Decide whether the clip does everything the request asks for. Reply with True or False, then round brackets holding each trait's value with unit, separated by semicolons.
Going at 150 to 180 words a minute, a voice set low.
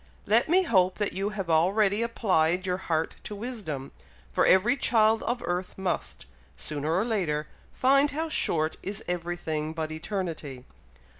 False (155 wpm; 185 Hz)